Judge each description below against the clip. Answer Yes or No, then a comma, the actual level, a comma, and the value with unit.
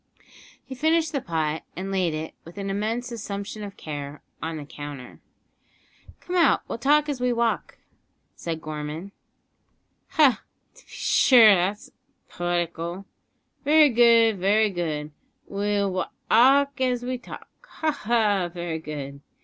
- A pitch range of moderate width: No, wide, 7.0 semitones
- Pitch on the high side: Yes, high, 200 Hz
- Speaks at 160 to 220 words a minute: No, slow, 135 wpm